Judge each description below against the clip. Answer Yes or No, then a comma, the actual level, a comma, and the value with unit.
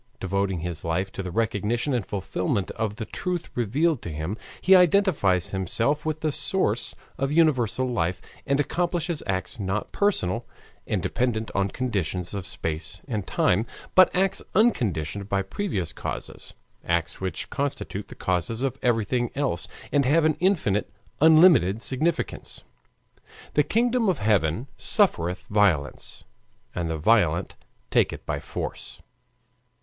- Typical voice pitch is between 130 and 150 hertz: No, low, 110 Hz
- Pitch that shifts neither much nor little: No, wide, 8.1 semitones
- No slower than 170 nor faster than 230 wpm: No, average, 140 wpm